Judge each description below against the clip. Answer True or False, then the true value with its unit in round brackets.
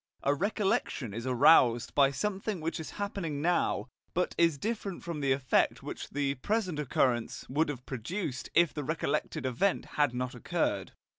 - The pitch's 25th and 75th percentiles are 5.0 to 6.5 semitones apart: True (5.4 semitones)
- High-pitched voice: False (145 Hz)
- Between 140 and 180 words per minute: True (160 wpm)